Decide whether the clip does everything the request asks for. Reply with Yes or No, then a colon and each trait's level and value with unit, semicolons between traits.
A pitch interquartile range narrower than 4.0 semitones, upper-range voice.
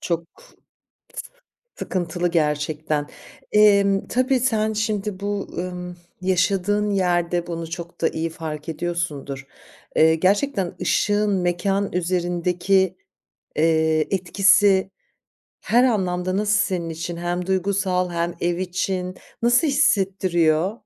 No: average, 2.8 semitones; medium, 180 Hz